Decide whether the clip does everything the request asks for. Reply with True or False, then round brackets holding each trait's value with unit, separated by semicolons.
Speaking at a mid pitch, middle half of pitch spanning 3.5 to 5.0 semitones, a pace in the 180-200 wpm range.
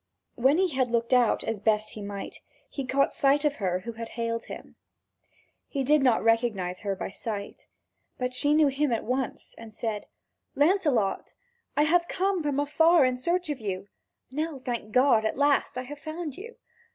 False (255 Hz; 4.7 semitones; 185 wpm)